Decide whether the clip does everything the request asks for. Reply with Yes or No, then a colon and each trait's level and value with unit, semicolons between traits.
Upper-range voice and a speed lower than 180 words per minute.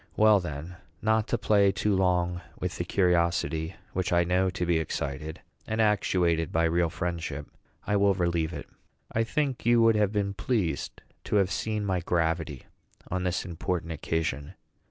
No: very low, 90 Hz; average, 165 wpm